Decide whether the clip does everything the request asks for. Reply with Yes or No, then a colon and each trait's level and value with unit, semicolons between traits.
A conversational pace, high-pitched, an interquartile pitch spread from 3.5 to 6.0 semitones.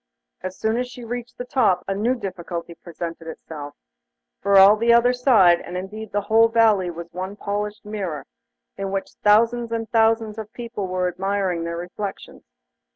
Yes: average, 170 wpm; high, 205 Hz; average, 3.9 semitones